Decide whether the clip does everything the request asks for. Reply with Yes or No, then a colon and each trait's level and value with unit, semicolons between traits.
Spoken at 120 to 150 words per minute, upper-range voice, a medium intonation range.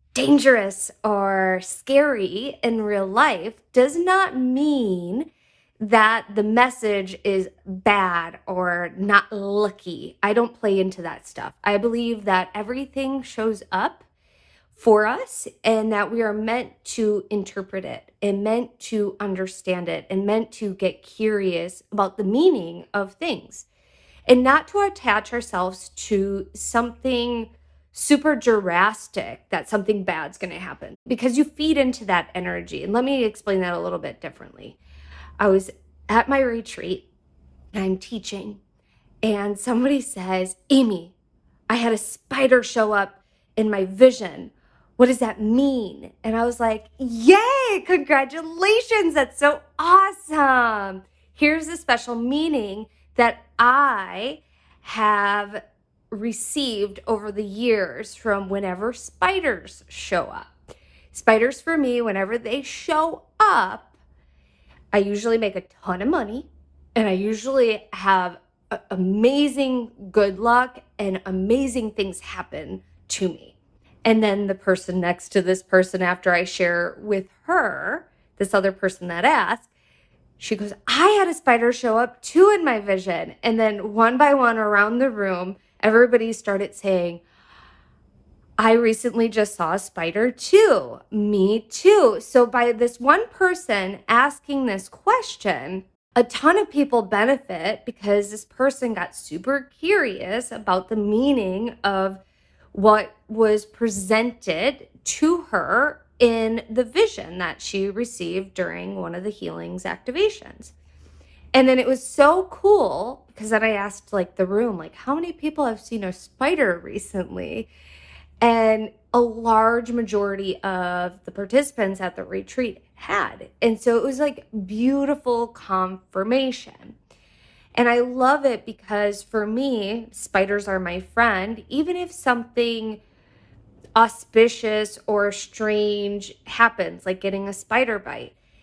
Yes: slow, 135 wpm; high, 220 Hz; average, 4.6 semitones